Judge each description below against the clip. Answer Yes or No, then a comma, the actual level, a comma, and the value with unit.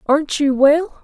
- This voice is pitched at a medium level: No, very high, 290 Hz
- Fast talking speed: No, average, 175 wpm